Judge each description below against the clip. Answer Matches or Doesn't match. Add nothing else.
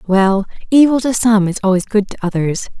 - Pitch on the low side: Doesn't match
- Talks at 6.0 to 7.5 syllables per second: Doesn't match